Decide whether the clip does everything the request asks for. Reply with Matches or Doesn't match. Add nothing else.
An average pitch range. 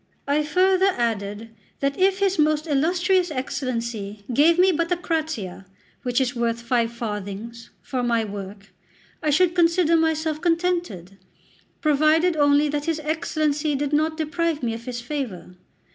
Doesn't match